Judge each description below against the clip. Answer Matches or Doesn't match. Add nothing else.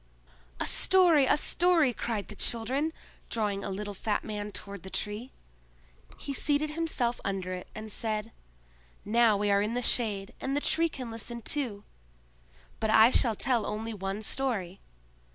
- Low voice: Doesn't match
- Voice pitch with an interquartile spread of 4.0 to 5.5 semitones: Matches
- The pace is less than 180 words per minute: Matches